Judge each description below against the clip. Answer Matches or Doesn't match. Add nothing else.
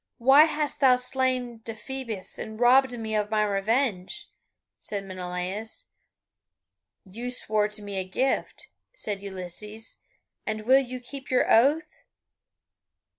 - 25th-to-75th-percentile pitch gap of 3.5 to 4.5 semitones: Matches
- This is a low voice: Doesn't match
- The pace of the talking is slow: Matches